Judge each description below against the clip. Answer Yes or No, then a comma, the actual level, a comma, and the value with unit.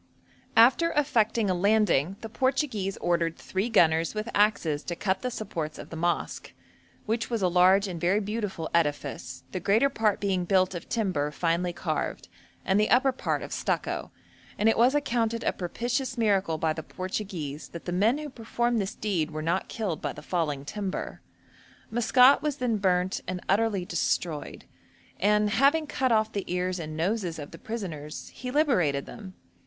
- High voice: Yes, high, 195 Hz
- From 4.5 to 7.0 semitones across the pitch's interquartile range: Yes, average, 4.8 semitones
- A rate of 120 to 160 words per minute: No, average, 175 wpm